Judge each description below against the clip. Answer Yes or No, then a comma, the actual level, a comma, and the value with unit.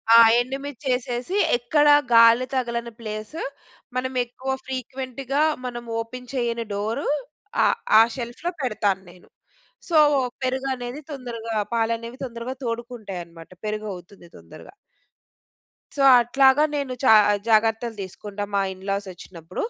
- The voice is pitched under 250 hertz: Yes, high, 235 Hz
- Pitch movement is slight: No, average, 3.2 semitones